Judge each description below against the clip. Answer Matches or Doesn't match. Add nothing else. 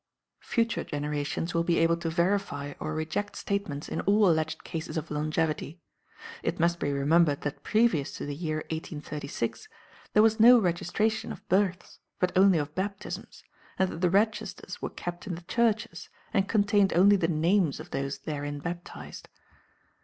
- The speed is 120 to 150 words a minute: Doesn't match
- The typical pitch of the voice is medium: Matches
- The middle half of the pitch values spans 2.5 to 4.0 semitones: Doesn't match